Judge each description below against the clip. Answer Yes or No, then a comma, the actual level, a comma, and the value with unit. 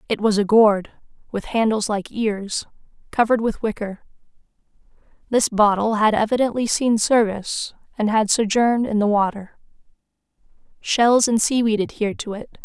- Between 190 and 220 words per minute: No, average, 140 wpm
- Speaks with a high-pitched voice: Yes, high, 220 Hz